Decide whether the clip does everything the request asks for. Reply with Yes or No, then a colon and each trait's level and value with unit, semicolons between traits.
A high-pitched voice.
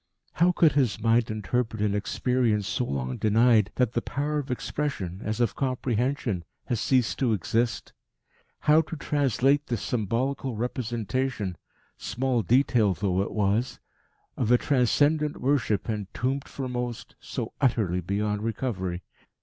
No: low, 120 Hz